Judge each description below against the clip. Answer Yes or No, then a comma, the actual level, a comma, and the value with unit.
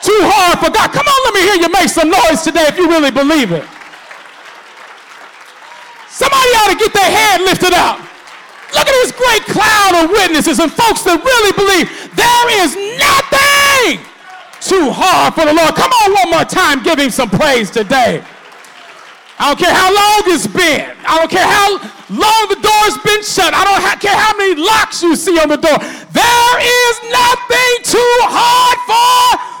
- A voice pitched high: Yes, very high, 390 Hz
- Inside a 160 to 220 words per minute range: Yes, average, 180 wpm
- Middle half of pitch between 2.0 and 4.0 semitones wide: No, average, 5.1 semitones